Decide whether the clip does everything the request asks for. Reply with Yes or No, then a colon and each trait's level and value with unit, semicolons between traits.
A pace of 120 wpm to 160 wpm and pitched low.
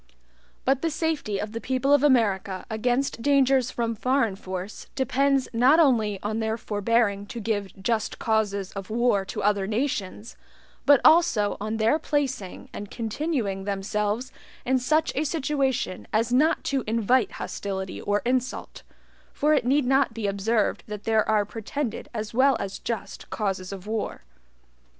No: average, 155 wpm; high, 225 Hz